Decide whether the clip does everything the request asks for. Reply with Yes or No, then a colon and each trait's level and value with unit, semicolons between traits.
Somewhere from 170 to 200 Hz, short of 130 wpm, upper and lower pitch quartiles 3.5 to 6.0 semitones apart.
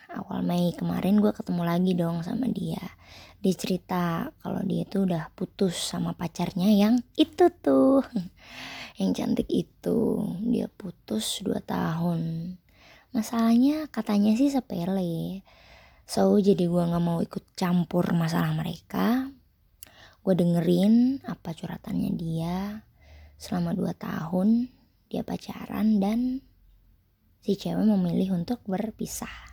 Yes: high, 190 Hz; average, 115 wpm; average, 4.0 semitones